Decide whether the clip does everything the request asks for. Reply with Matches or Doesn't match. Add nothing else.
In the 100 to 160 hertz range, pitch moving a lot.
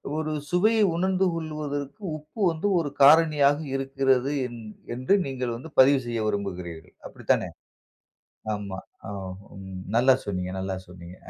Matches